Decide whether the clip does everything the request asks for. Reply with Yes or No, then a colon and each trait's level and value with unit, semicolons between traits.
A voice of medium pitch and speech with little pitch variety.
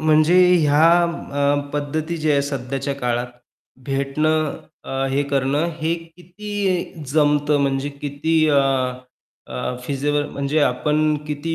Yes: medium, 145 Hz; narrow, 2.1 semitones